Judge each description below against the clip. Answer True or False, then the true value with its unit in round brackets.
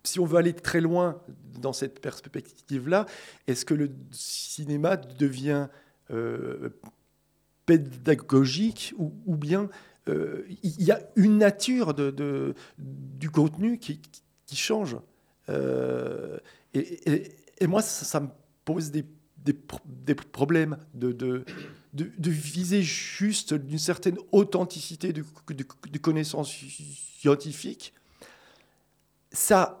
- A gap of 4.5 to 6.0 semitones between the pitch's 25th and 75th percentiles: False (3.9 semitones)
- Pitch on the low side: False (150 Hz)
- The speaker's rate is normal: False (120 wpm)